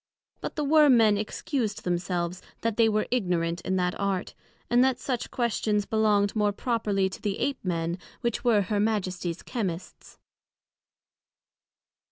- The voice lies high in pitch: Yes, high, 210 Hz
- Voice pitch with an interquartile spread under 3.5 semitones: No, average, 4.1 semitones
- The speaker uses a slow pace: No, average, 145 wpm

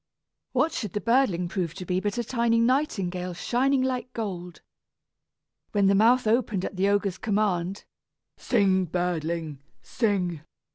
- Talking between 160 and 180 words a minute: No, average, 140 wpm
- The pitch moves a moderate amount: Yes, average, 4.5 semitones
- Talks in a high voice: Yes, high, 200 Hz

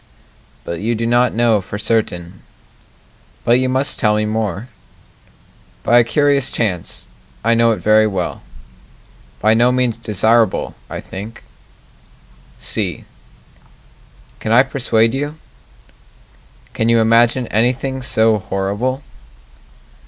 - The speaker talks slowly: Yes, slow, 115 wpm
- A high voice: No, low, 115 Hz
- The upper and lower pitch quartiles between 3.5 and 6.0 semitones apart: No, narrow, 2.5 semitones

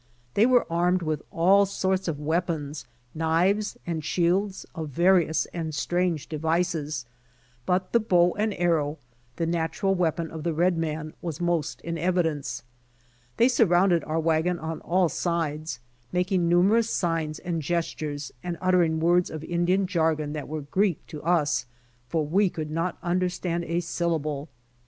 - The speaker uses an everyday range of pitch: No, narrow, 2.3 semitones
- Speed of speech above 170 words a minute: No, average, 150 wpm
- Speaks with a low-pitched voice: No, medium, 170 Hz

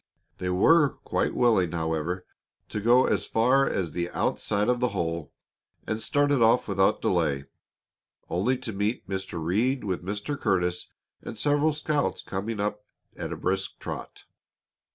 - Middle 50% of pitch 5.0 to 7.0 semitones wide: Yes, wide, 5.5 semitones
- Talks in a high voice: No, low, 105 Hz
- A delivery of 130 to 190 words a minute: Yes, average, 150 wpm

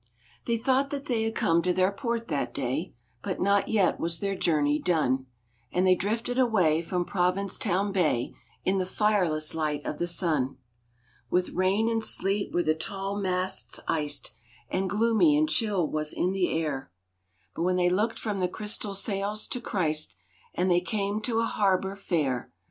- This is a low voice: No, medium, 185 Hz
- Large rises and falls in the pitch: No, average, 4.2 semitones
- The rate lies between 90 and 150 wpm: No, average, 165 wpm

